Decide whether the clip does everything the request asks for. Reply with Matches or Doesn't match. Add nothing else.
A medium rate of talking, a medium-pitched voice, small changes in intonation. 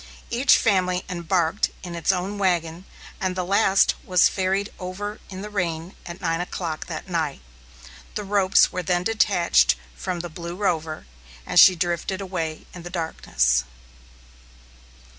Matches